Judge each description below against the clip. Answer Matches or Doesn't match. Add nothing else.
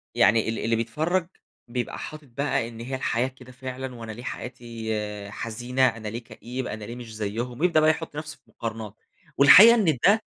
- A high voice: Doesn't match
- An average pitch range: Matches